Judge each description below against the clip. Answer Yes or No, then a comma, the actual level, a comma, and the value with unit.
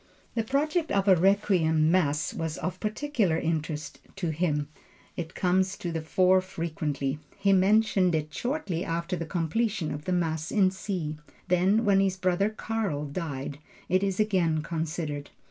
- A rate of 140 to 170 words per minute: Yes, average, 155 wpm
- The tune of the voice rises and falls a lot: No, average, 3.8 semitones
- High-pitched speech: No, medium, 180 Hz